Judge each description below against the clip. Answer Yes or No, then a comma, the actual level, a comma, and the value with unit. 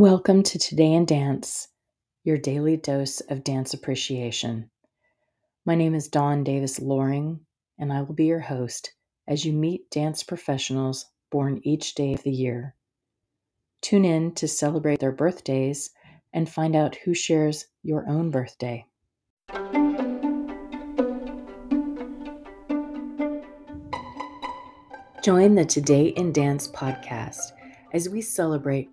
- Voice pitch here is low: No, medium, 155 Hz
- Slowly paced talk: Yes, slow, 120 wpm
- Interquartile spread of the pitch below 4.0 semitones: No, average, 5.2 semitones